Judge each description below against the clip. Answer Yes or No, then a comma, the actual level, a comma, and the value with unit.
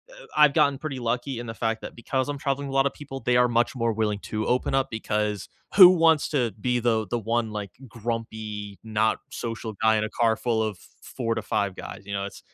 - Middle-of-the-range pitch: No, low, 115 Hz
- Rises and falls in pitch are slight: No, average, 3.3 semitones